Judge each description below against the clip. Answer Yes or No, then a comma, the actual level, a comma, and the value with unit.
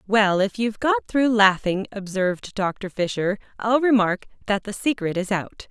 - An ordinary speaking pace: Yes, average, 170 wpm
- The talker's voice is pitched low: No, high, 210 Hz